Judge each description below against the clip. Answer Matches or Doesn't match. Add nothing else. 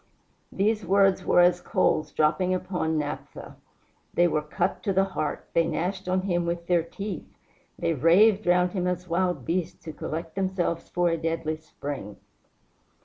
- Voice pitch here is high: Doesn't match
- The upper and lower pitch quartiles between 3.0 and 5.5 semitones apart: Doesn't match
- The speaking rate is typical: Matches